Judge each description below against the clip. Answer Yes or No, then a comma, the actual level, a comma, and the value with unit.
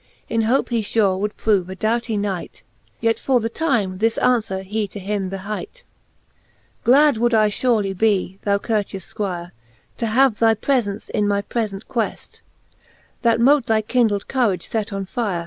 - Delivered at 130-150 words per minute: No, average, 170 wpm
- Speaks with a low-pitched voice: No, high, 215 Hz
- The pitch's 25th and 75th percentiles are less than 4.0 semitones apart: Yes, average, 2.9 semitones